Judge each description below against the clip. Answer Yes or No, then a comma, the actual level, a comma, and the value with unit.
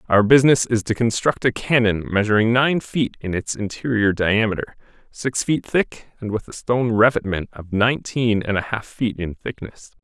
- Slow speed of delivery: No, average, 180 wpm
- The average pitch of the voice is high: No, low, 110 Hz